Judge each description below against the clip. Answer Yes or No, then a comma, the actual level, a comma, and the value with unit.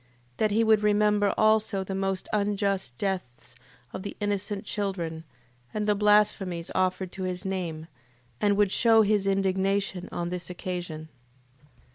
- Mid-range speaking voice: No, high, 195 Hz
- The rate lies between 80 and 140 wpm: Yes, slow, 135 wpm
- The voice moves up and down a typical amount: No, narrow, 2.3 semitones